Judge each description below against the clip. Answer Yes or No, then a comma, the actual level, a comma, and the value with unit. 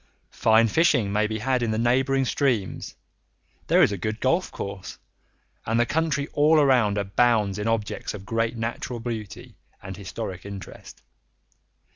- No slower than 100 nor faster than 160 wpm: Yes, average, 150 wpm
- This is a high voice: No, low, 115 Hz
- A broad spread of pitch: No, average, 3.8 semitones